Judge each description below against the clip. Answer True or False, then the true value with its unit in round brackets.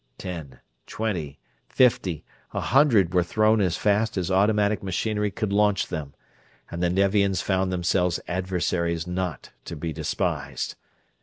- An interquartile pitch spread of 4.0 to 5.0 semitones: False (3.2 semitones)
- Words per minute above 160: False (135 wpm)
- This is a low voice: True (95 Hz)